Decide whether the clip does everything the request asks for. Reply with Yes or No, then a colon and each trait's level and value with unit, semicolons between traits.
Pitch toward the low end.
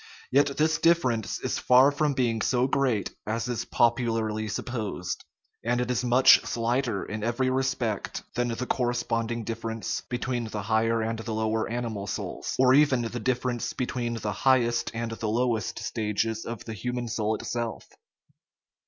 Yes: low, 120 Hz